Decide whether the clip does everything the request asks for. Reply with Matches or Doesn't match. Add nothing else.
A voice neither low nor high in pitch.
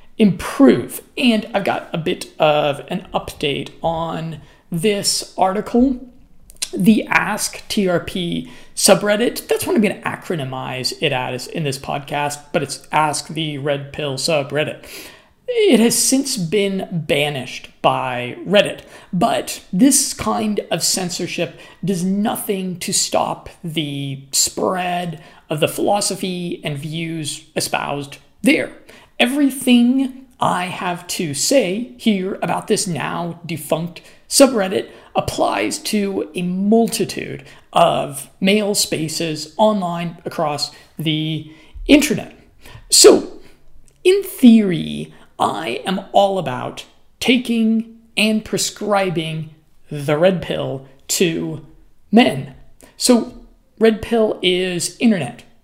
Matches